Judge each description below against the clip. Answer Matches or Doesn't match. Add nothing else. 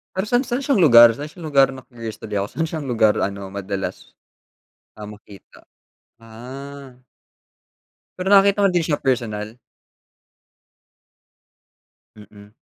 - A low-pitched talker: Matches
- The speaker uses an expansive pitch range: Matches